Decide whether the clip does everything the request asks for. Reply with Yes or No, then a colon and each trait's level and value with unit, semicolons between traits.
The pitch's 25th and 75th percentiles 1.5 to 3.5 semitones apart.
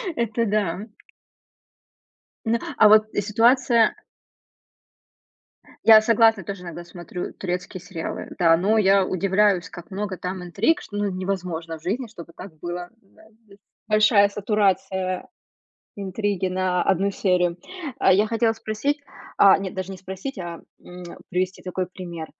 Yes: average, 2.8 semitones